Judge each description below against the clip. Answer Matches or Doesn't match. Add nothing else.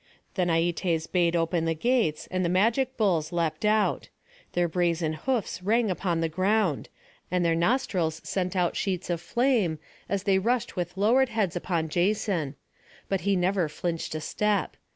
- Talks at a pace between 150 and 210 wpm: Matches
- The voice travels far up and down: Doesn't match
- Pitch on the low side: Doesn't match